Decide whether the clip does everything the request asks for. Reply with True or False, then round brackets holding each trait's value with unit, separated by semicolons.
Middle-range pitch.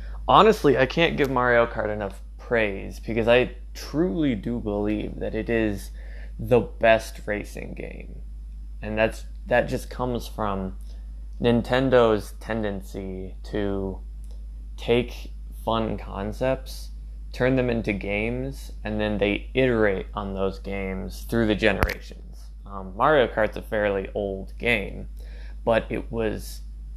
False (100 Hz)